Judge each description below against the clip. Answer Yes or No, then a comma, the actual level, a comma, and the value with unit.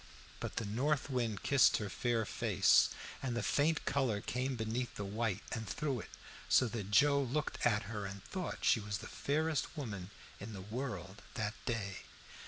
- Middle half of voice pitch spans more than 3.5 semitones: Yes, average, 4.6 semitones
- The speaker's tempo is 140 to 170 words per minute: No, average, 180 wpm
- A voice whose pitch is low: Yes, low, 115 Hz